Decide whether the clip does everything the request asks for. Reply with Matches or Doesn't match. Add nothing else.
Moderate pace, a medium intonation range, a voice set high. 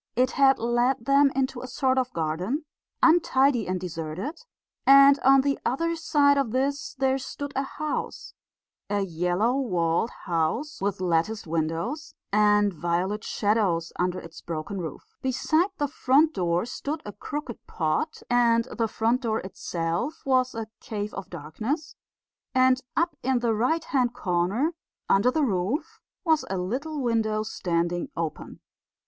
Doesn't match